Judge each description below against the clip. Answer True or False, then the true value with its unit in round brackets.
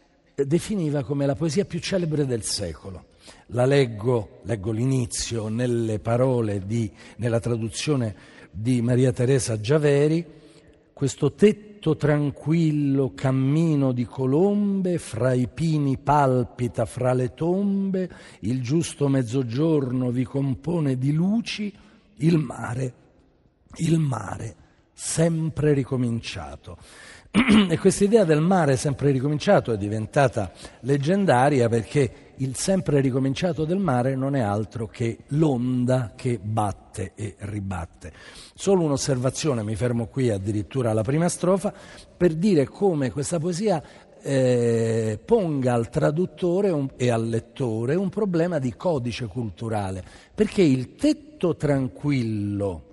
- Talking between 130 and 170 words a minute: False (115 wpm)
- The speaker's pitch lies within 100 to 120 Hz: False (135 Hz)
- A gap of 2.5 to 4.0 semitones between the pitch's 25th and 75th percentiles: False (5.5 semitones)